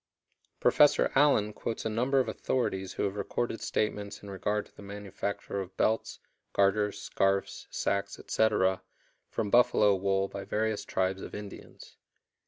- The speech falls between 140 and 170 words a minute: Yes, average, 145 wpm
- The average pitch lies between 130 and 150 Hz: No, low, 100 Hz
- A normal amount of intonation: No, narrow, 2.1 semitones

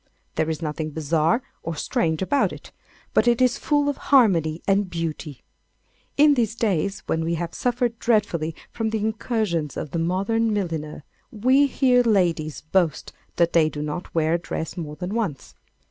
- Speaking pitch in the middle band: Yes, medium, 175 Hz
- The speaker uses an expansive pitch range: Yes, wide, 6.1 semitones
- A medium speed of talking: Yes, average, 170 wpm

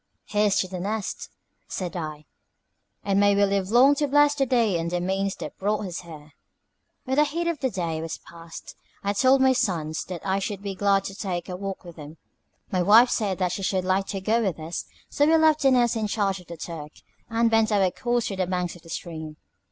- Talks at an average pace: No, fast, 230 wpm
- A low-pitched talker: No, high, 195 Hz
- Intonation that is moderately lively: Yes, average, 4.4 semitones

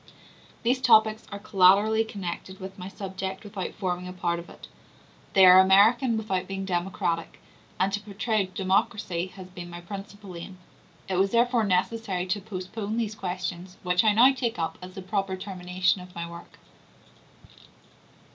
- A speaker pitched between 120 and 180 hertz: No, high, 190 Hz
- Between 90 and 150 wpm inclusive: No, average, 160 wpm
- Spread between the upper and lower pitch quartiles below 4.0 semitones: Yes, narrow, 2.5 semitones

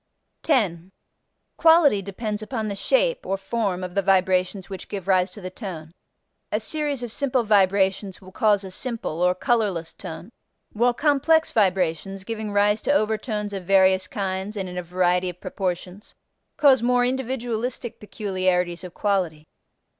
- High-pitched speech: Yes, high, 200 Hz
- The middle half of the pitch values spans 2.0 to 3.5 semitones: No, average, 3.9 semitones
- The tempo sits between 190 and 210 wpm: No, average, 155 wpm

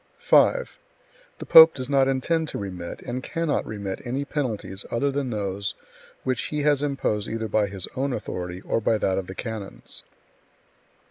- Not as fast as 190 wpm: Yes, average, 170 wpm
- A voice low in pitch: Yes, low, 120 Hz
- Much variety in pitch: Yes, wide, 5.9 semitones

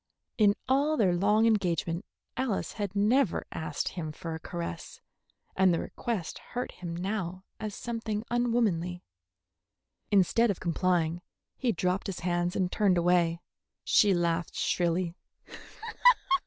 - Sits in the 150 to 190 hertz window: Yes, medium, 185 Hz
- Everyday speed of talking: No, slow, 130 wpm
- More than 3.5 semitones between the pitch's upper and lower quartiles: Yes, average, 4.0 semitones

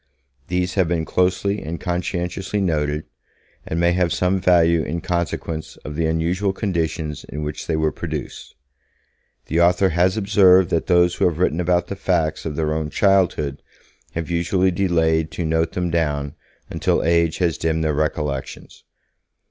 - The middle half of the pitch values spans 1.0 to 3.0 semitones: Yes, narrow, 2.4 semitones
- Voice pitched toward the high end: No, very low, 85 Hz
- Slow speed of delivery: No, average, 160 wpm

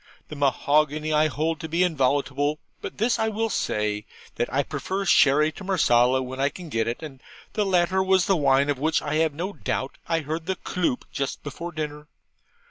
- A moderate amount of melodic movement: Yes, average, 4.0 semitones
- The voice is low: No, medium, 155 Hz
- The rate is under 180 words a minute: No, average, 200 wpm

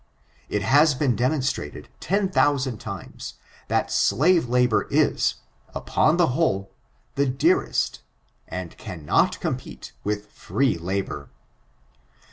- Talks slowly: Yes, slow, 105 wpm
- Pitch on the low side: Yes, low, 125 Hz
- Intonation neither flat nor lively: No, wide, 6.7 semitones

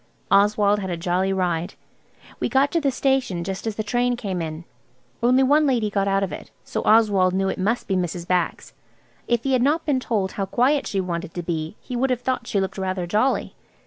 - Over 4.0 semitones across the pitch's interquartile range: Yes, average, 5.1 semitones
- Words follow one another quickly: Yes, fast, 220 wpm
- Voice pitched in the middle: No, high, 200 Hz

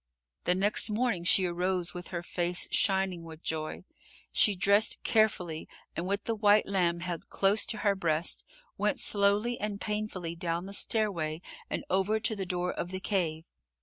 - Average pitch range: Yes, average, 3.0 semitones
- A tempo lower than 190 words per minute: Yes, average, 170 wpm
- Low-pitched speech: No, medium, 185 Hz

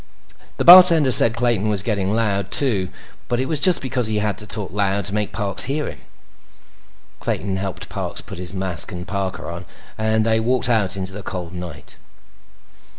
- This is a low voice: Yes, low, 105 Hz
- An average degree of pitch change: Yes, average, 3.8 semitones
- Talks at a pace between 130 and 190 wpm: Yes, average, 185 wpm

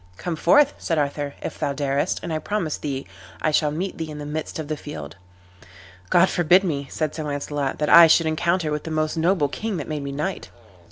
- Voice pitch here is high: No, medium, 155 Hz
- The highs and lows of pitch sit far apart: No, narrow, 2.6 semitones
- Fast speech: Yes, fast, 220 wpm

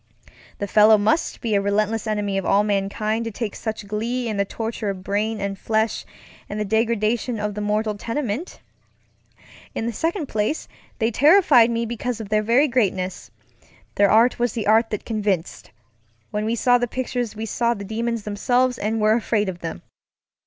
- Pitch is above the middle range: Yes, high, 215 Hz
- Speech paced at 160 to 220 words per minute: Yes, average, 175 wpm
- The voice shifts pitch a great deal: No, narrow, 2.4 semitones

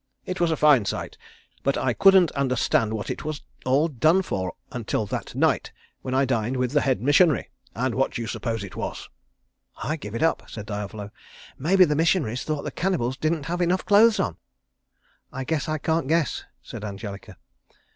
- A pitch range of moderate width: No, wide, 6.1 semitones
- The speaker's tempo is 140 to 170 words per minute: No, average, 185 wpm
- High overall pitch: No, low, 135 Hz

